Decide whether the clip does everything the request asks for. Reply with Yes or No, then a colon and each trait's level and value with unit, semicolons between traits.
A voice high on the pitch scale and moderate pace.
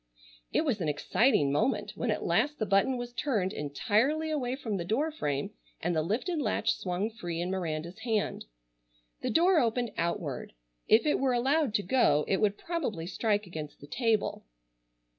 Yes: high, 215 Hz; average, 175 wpm